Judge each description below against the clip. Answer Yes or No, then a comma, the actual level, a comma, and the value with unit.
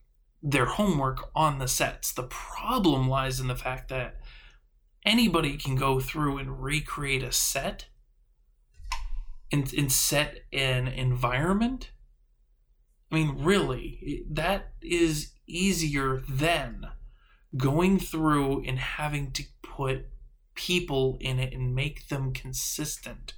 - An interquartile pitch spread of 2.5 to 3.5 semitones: Yes, average, 2.9 semitones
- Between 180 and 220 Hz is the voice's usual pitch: No, low, 135 Hz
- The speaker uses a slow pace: Yes, slow, 115 wpm